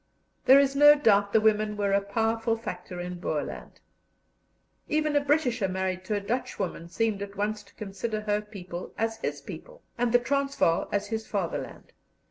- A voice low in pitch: No, high, 215 Hz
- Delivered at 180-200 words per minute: No, average, 170 wpm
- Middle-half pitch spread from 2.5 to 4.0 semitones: Yes, average, 3.2 semitones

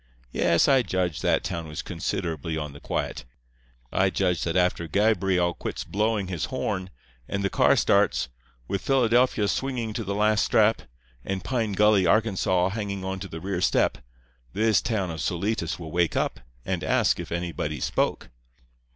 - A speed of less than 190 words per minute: Yes, average, 160 wpm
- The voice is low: Yes, very low, 95 Hz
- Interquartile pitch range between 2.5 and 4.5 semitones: Yes, average, 3.8 semitones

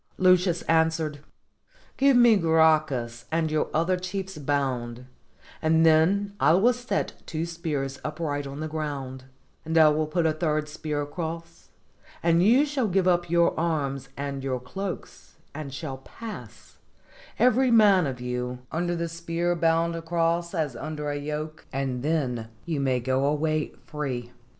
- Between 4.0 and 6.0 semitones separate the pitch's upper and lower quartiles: No, average, 3.5 semitones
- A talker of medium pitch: Yes, medium, 160 Hz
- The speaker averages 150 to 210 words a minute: Yes, average, 155 wpm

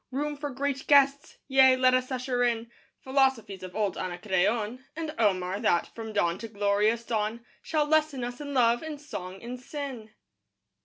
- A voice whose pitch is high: Yes, high, 245 Hz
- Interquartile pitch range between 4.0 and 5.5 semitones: Yes, average, 4.6 semitones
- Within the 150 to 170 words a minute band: Yes, average, 165 wpm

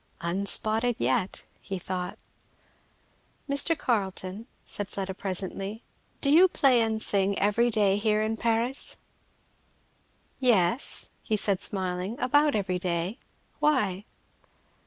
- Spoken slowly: Yes, slow, 110 wpm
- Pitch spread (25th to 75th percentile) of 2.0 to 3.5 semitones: No, average, 3.9 semitones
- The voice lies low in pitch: No, high, 210 Hz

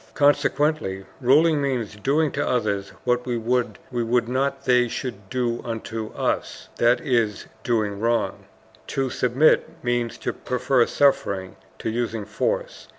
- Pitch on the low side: Yes, low, 120 Hz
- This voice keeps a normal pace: No, slow, 130 wpm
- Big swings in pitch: No, average, 3.2 semitones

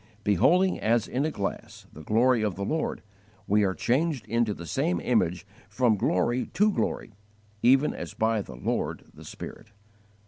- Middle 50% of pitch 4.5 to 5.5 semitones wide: Yes, average, 4.9 semitones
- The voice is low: Yes, low, 115 Hz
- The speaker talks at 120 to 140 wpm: No, average, 165 wpm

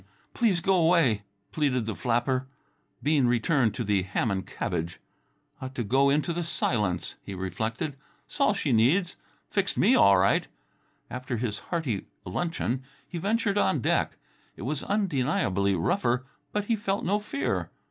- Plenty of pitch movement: Yes, wide, 8.0 semitones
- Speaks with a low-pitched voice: Yes, low, 130 Hz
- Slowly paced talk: No, average, 155 wpm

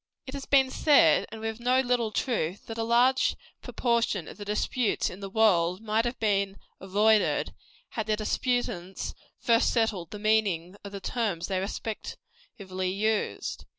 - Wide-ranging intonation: No, average, 3.3 semitones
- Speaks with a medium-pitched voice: No, high, 215 Hz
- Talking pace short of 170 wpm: Yes, average, 155 wpm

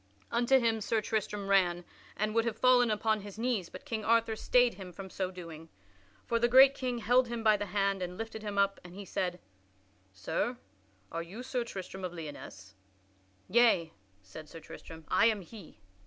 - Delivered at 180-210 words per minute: Yes, average, 185 wpm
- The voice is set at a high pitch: Yes, high, 210 Hz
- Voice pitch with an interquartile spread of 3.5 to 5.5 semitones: Yes, average, 4.3 semitones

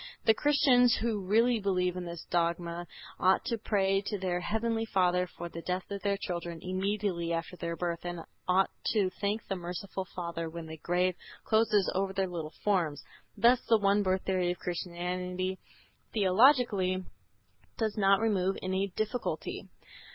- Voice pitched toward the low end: No, high, 190 Hz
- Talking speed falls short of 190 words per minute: Yes, average, 160 wpm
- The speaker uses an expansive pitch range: No, average, 3.0 semitones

